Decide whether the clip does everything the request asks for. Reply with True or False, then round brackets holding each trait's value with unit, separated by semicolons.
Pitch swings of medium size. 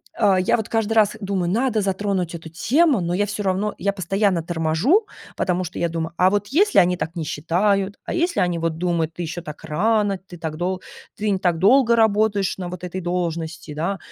True (3.4 semitones)